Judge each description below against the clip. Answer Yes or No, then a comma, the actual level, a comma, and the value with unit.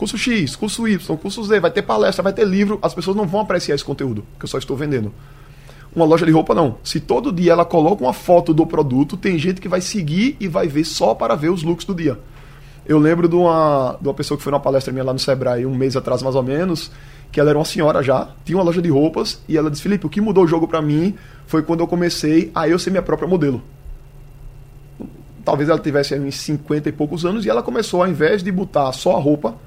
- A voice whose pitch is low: No, medium, 155 Hz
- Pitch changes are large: No, average, 4.4 semitones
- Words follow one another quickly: Yes, fast, 250 wpm